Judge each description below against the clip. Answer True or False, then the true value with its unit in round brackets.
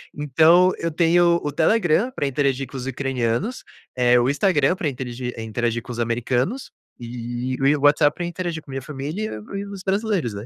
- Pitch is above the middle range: False (145 Hz)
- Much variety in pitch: True (5.9 semitones)